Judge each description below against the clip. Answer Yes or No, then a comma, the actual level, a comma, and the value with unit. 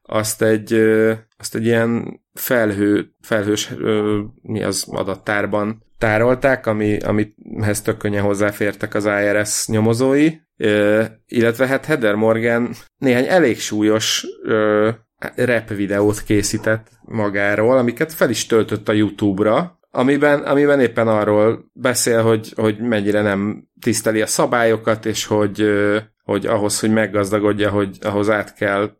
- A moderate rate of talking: Yes, average, 130 wpm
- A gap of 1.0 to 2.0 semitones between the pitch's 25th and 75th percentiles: Yes, narrow, 1.6 semitones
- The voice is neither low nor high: No, low, 110 Hz